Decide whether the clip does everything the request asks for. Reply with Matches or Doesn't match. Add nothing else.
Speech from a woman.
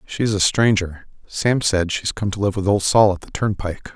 Doesn't match